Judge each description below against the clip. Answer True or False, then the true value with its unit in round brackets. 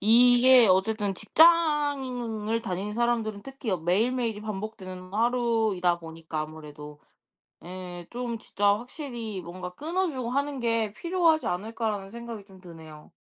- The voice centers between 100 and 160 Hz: False (220 Hz)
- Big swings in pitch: False (4.9 semitones)